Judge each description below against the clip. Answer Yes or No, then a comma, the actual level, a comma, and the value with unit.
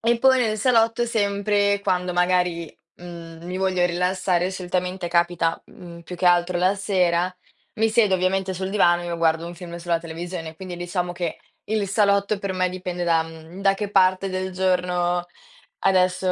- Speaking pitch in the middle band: Yes, medium, 180 Hz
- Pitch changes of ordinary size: No, narrow, 2.0 semitones